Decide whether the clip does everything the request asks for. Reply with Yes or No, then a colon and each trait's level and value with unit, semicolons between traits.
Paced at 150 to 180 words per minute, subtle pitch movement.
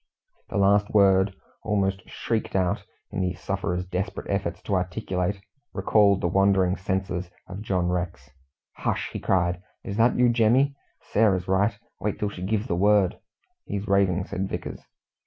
Yes: average, 155 wpm; narrow, 2.1 semitones